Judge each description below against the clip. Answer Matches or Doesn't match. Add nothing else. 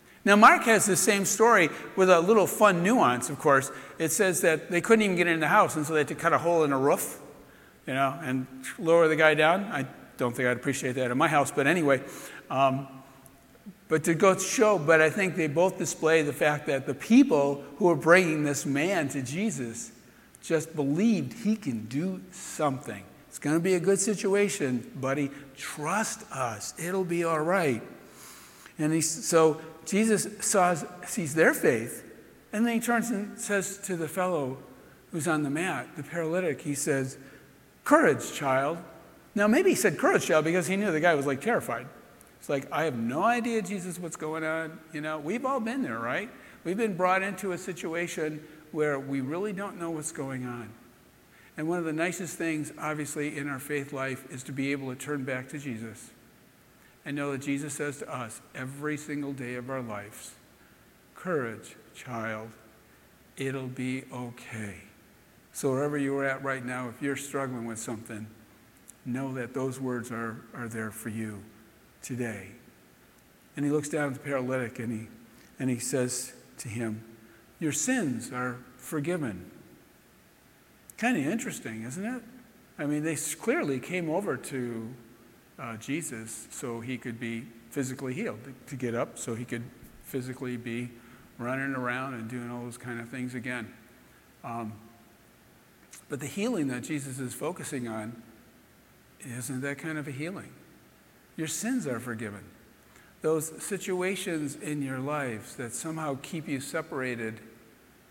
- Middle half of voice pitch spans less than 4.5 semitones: Doesn't match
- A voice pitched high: Doesn't match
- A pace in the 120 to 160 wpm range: Doesn't match